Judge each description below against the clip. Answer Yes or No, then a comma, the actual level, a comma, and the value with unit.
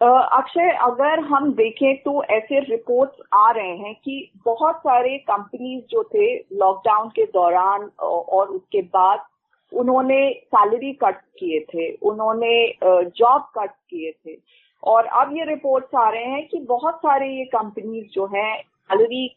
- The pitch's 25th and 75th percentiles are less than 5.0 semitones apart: No, wide, 5.4 semitones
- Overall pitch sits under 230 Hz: No, very high, 250 Hz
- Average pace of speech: Yes, average, 145 wpm